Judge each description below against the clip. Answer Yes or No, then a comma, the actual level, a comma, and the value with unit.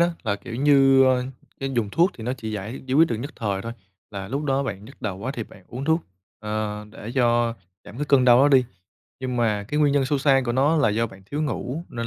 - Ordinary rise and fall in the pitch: Yes, average, 4.1 semitones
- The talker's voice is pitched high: No, low, 125 Hz